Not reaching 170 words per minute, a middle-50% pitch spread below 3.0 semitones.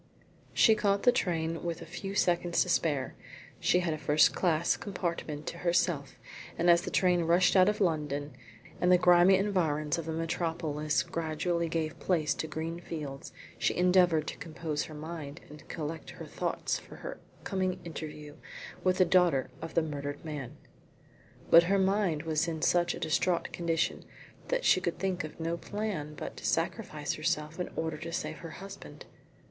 No: average, 175 wpm; narrow, 2.6 semitones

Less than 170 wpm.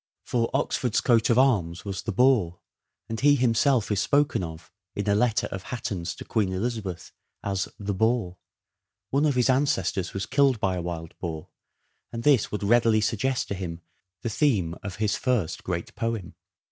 No: average, 180 wpm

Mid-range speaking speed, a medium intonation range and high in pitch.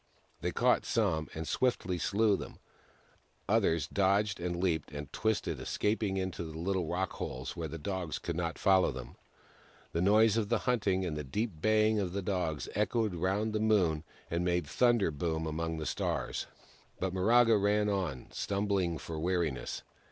No: average, 160 wpm; average, 4.2 semitones; very low, 95 Hz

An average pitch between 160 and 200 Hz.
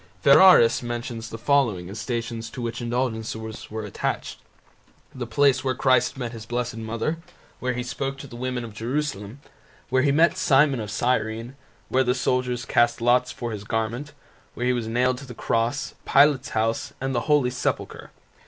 No: low, 120 Hz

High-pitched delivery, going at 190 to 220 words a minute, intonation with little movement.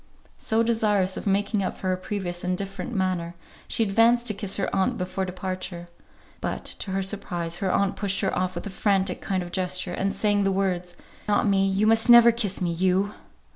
Yes: high, 195 Hz; fast, 205 wpm; narrow, 2.0 semitones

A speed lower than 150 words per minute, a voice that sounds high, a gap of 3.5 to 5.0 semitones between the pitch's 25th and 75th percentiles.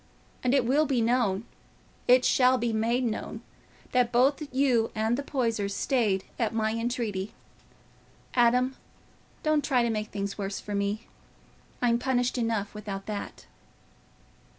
No: slow, 135 wpm; high, 235 Hz; average, 3.0 semitones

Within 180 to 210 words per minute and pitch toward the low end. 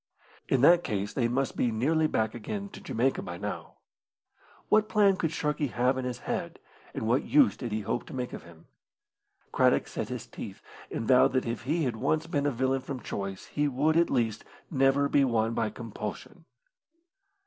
Yes: average, 190 wpm; low, 130 Hz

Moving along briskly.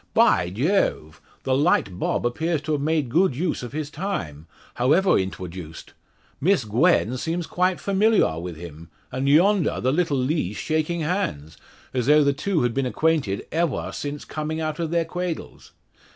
No: average, 165 wpm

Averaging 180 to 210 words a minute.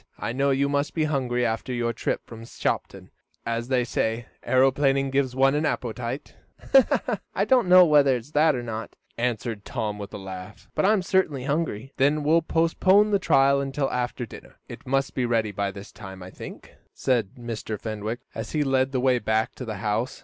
Yes: average, 195 wpm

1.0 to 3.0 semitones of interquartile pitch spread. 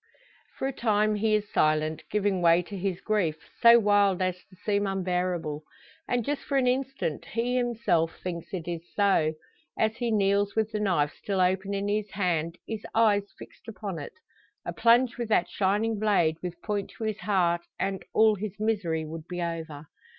No: average, 3.8 semitones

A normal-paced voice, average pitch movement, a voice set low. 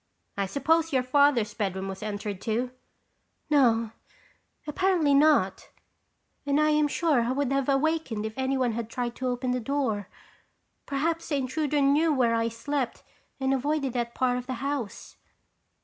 No: average, 165 wpm; average, 3.8 semitones; very high, 260 Hz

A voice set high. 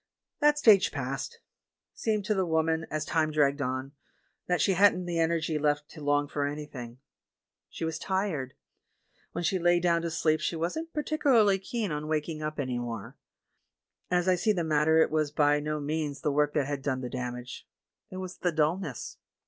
No: medium, 155 Hz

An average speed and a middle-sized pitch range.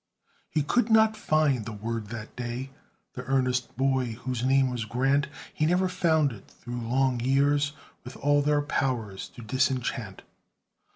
Yes: average, 155 wpm; average, 3.3 semitones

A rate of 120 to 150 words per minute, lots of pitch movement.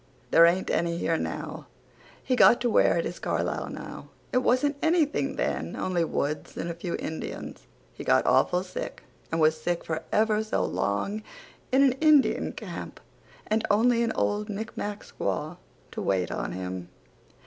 No: average, 165 wpm; wide, 6.3 semitones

